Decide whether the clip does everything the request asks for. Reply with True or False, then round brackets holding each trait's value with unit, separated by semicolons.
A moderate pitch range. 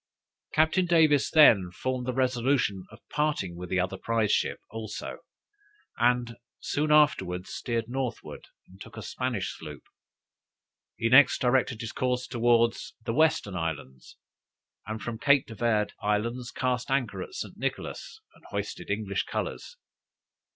True (4.0 semitones)